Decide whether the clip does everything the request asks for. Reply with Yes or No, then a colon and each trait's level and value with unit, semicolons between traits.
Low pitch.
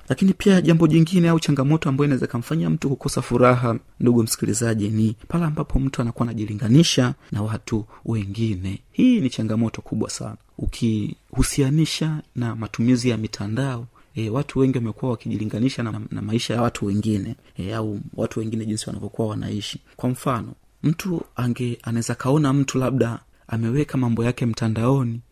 Yes: low, 120 Hz